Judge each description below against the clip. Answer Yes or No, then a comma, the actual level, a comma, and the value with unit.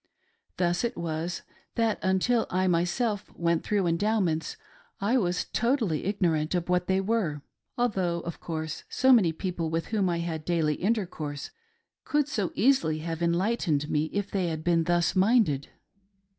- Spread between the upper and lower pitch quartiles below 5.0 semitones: Yes, average, 4.2 semitones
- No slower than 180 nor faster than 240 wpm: No, average, 155 wpm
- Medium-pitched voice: Yes, medium, 175 Hz